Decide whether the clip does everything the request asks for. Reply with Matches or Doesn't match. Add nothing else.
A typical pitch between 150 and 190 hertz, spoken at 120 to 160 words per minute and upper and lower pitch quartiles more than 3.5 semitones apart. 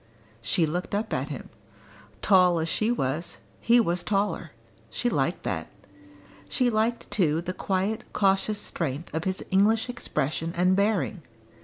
Matches